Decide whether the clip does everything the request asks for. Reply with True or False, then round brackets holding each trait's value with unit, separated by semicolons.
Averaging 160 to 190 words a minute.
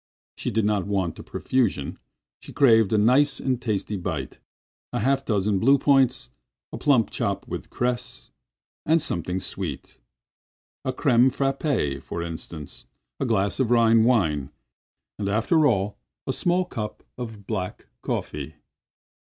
False (135 wpm)